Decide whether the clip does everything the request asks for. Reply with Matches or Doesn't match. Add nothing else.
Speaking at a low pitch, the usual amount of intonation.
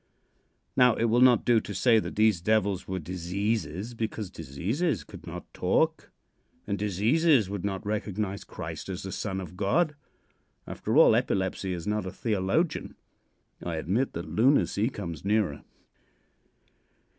Matches